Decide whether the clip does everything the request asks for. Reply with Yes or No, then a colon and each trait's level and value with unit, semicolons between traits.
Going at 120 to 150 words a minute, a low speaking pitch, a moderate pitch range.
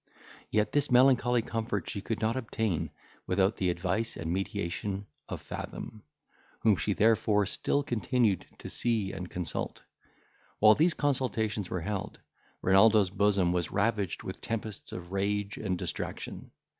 Yes: average, 140 wpm; low, 105 Hz; average, 3.0 semitones